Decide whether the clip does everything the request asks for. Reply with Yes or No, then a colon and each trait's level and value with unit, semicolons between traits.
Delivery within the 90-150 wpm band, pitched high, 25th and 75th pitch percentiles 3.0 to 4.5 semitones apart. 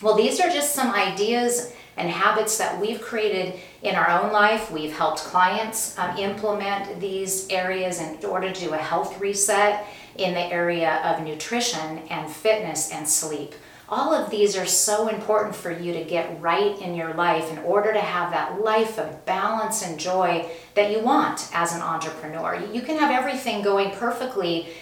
No: average, 180 wpm; high, 195 Hz; average, 4.2 semitones